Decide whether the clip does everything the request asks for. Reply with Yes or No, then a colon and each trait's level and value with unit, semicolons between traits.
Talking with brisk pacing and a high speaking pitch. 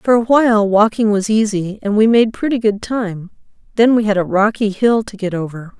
Yes: fast, 215 wpm; high, 210 Hz